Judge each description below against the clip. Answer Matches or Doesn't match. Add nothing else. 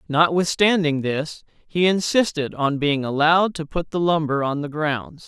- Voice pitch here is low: Doesn't match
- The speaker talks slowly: Doesn't match